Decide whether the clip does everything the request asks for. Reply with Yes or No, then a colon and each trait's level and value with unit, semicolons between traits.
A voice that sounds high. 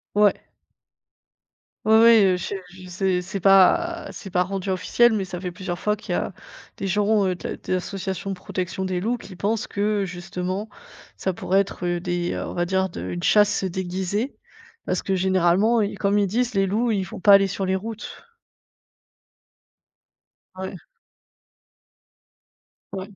Yes: high, 195 Hz